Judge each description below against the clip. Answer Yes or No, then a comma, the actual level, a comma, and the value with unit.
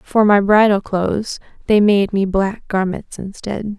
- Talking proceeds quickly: No, average, 160 wpm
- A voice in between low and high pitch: No, high, 200 Hz